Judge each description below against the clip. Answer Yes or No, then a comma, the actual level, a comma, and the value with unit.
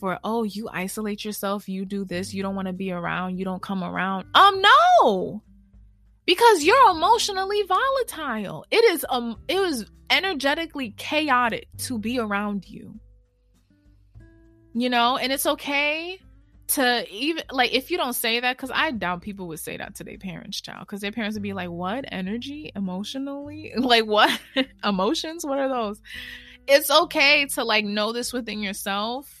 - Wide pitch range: Yes, wide, 6.7 semitones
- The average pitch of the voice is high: Yes, high, 230 Hz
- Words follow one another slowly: No, average, 165 wpm